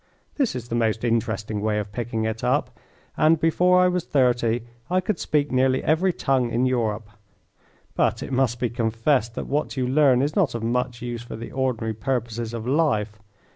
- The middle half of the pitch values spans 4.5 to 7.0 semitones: No, average, 3.9 semitones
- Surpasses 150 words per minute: Yes, average, 190 wpm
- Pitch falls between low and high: No, low, 120 Hz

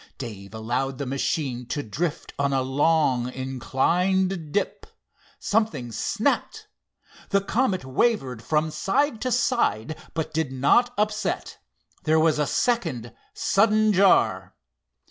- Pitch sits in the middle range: Yes, medium, 155 Hz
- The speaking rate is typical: No, slow, 120 wpm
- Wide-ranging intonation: Yes, wide, 7.3 semitones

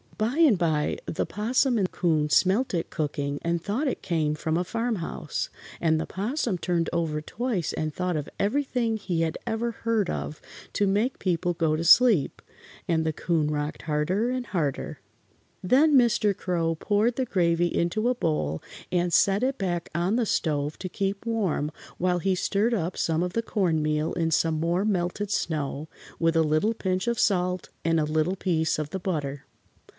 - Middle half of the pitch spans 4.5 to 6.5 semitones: Yes, average, 5.0 semitones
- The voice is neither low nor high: Yes, medium, 180 Hz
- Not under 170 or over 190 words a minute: Yes, average, 180 wpm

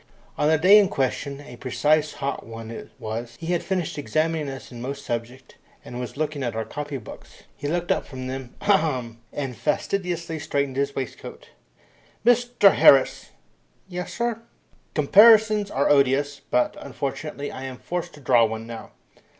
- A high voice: No, medium, 140 Hz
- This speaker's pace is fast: No, average, 165 wpm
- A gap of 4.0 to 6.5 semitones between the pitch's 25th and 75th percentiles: Yes, average, 4.7 semitones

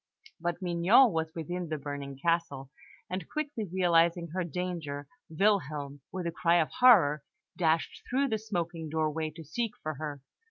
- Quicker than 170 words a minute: No, average, 155 wpm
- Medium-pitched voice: Yes, medium, 170 Hz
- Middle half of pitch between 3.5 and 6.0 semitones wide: No, average, 3.1 semitones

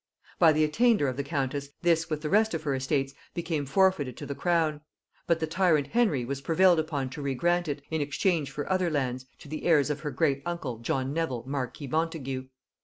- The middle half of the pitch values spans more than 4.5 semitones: No, average, 3.5 semitones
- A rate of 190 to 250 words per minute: Yes, fast, 205 wpm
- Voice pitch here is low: No, medium, 150 Hz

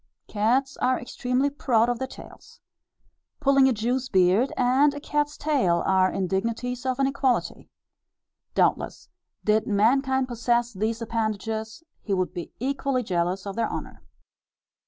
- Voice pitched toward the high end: Yes, high, 240 Hz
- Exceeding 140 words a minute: No, slow, 135 wpm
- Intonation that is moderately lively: Yes, average, 3.9 semitones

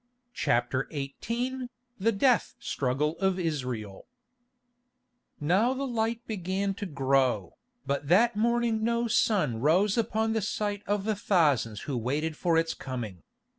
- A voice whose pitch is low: No, medium, 185 Hz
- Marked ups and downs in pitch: Yes, wide, 8.2 semitones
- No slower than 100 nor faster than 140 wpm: Yes, slow, 135 wpm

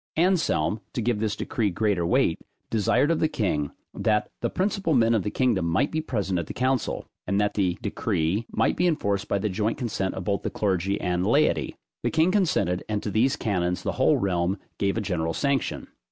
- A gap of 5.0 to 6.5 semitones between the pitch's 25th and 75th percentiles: Yes, wide, 5.5 semitones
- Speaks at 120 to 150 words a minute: No, fast, 205 wpm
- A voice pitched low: Yes, low, 105 Hz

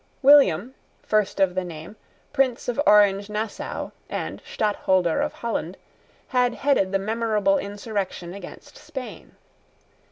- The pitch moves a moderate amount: Yes, average, 4.5 semitones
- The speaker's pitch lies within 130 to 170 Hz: No, high, 210 Hz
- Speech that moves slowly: Yes, slow, 120 wpm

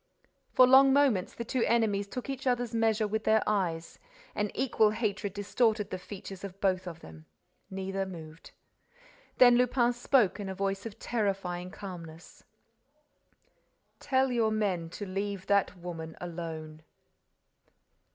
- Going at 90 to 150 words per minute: Yes, average, 140 wpm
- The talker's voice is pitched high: Yes, high, 200 Hz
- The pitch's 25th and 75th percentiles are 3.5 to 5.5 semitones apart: Yes, average, 4.1 semitones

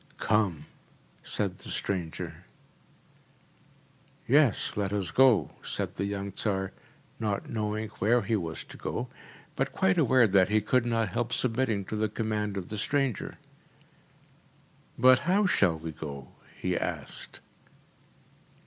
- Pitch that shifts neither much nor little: Yes, average, 3.6 semitones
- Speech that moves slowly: Yes, slow, 130 wpm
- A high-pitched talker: No, low, 105 Hz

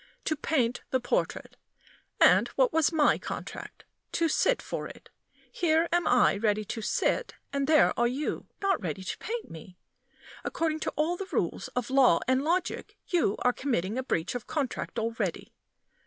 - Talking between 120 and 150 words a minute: No, average, 170 wpm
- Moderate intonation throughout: No, wide, 6.0 semitones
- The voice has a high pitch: Yes, very high, 275 Hz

